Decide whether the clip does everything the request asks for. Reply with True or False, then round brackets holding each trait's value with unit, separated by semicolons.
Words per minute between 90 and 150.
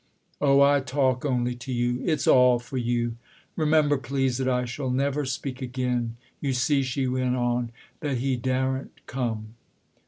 False (180 wpm)